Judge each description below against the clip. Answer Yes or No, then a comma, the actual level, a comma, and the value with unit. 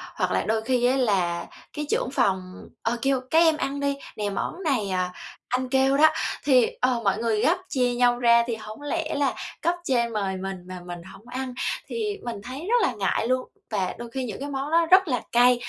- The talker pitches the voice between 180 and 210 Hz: No, high, 245 Hz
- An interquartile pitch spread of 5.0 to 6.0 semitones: No, average, 4.6 semitones